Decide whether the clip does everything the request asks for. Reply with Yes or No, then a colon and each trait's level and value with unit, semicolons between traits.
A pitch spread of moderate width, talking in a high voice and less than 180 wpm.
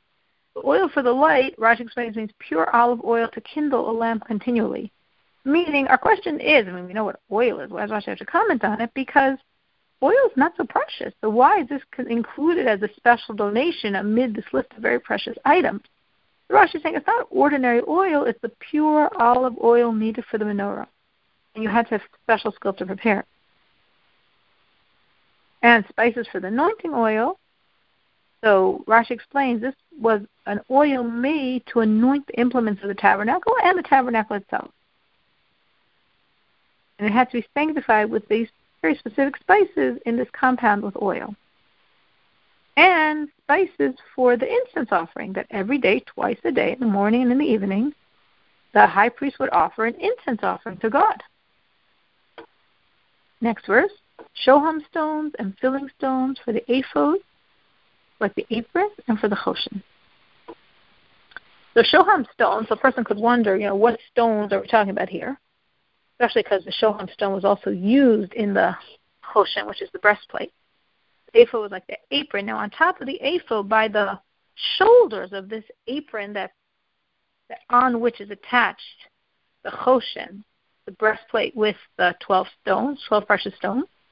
Yes: average, 4.6 semitones; high, 235 Hz; average, 170 wpm